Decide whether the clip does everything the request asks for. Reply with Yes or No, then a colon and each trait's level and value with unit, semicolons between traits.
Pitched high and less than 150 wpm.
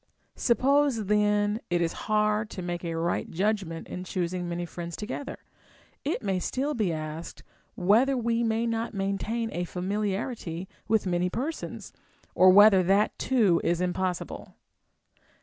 Yes: high, 200 Hz; average, 140 wpm